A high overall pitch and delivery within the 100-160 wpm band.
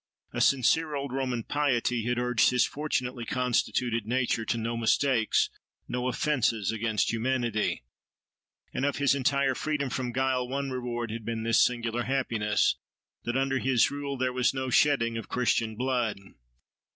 No: low, 125 Hz; average, 150 wpm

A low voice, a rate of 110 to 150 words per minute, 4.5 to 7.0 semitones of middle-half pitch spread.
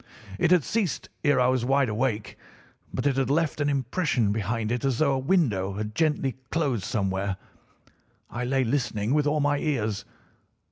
No: low, 130 Hz; average, 175 wpm; average, 4.9 semitones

